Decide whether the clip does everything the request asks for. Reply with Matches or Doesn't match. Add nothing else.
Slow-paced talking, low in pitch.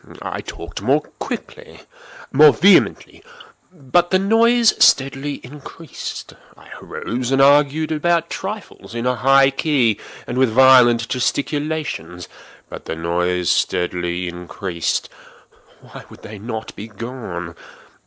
Matches